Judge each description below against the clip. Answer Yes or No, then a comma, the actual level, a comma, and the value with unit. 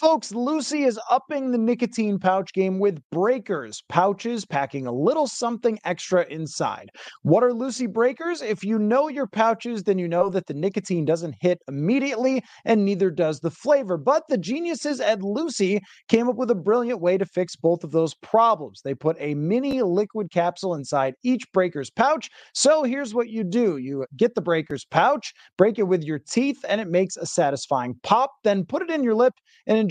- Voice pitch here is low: No, high, 210 Hz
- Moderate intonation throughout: No, wide, 6.3 semitones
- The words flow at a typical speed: Yes, average, 195 wpm